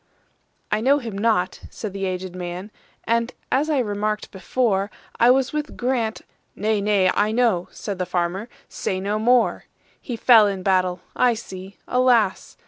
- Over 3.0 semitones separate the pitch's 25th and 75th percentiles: Yes, average, 4.0 semitones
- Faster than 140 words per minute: No, slow, 135 wpm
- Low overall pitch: No, high, 210 Hz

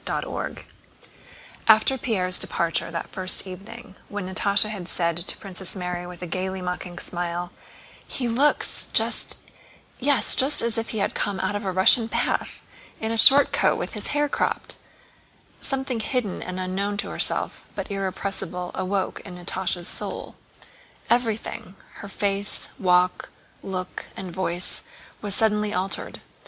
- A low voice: No, high, 195 Hz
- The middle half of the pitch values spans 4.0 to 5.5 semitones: No, average, 3.3 semitones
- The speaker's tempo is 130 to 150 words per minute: Yes, average, 145 wpm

